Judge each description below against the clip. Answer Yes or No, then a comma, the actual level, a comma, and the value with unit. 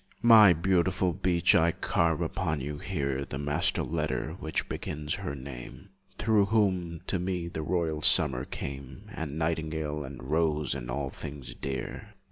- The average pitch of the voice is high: No, very low, 80 Hz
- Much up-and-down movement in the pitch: No, average, 3.7 semitones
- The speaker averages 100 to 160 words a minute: Yes, average, 150 wpm